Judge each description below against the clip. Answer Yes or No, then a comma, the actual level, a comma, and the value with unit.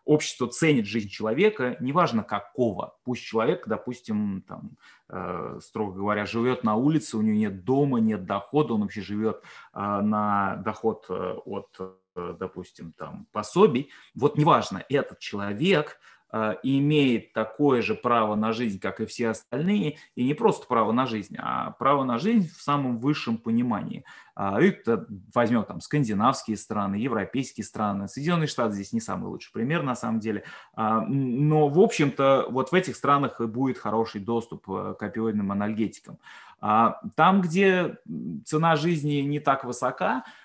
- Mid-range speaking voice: No, low, 115 Hz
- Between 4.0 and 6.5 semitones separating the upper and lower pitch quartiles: Yes, average, 5.3 semitones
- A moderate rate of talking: Yes, average, 145 wpm